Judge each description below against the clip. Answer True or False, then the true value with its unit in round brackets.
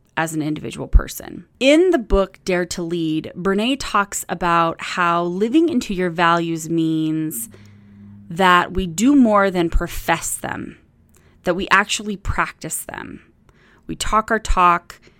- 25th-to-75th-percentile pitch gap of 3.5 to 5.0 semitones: True (4.1 semitones)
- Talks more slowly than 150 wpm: True (140 wpm)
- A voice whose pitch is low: False (175 Hz)